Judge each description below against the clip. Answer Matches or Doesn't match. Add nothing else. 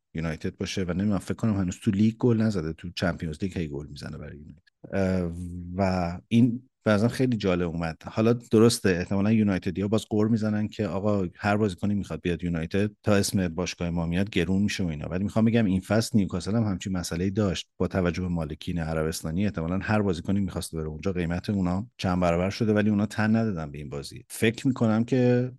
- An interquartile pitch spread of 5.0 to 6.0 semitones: Doesn't match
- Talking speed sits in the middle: Doesn't match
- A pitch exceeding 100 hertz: Doesn't match